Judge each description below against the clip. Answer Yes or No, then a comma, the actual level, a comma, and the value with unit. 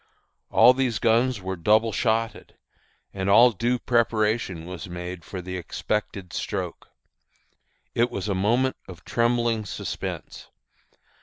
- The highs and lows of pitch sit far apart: No, average, 4.0 semitones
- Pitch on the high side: No, low, 110 Hz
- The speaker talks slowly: Yes, slow, 125 wpm